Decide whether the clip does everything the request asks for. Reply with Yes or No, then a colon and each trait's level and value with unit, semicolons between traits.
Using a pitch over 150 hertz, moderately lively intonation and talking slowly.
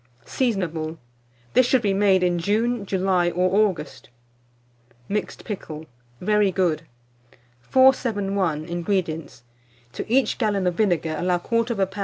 Yes: high, 190 Hz; average, 3.6 semitones; slow, 120 wpm